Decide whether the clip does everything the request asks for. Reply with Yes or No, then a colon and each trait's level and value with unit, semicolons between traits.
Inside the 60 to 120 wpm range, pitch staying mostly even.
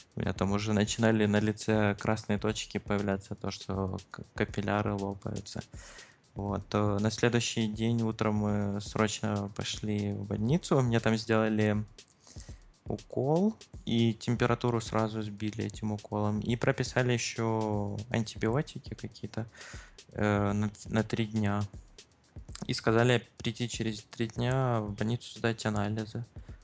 Yes: average, 115 wpm; narrow, 1.9 semitones